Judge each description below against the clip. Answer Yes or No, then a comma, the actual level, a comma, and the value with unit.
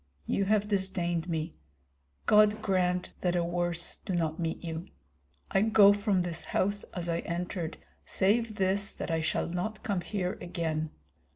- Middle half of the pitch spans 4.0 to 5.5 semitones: No, average, 3.0 semitones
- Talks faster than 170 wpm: No, average, 160 wpm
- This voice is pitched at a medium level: Yes, medium, 180 Hz